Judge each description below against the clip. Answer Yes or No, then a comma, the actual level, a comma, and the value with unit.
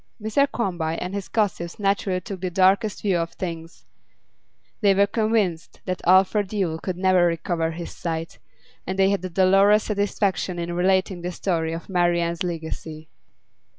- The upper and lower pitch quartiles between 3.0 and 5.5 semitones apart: No, narrow, 2.6 semitones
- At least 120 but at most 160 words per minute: Yes, average, 155 wpm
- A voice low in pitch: No, medium, 185 Hz